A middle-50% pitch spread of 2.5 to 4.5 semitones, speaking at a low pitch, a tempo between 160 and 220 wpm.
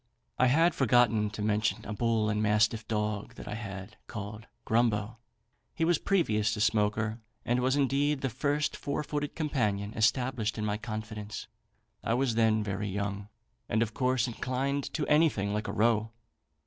Yes: average, 3.4 semitones; low, 110 Hz; average, 165 wpm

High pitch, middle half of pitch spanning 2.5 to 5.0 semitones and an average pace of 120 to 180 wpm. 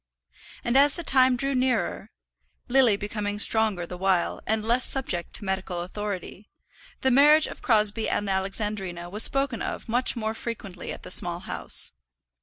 Yes: high, 215 Hz; average, 4.7 semitones; average, 160 wpm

